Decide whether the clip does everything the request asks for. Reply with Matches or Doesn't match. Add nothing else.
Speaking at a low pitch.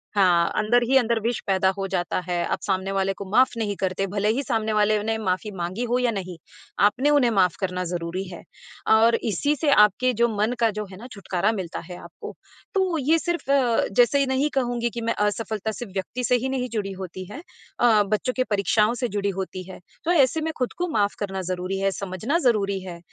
Doesn't match